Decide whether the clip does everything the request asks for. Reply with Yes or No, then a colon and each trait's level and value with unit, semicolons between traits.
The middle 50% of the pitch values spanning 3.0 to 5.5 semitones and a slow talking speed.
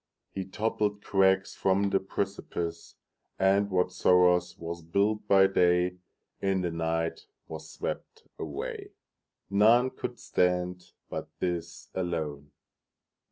No: narrow, 2.5 semitones; slow, 95 wpm